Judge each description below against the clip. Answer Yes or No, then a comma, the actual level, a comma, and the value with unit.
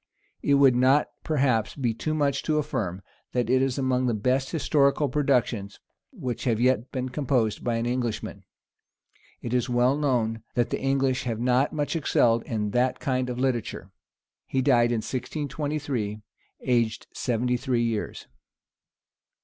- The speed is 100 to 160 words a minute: Yes, average, 150 wpm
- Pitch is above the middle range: No, low, 125 Hz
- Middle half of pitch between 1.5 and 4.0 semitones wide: Yes, average, 2.8 semitones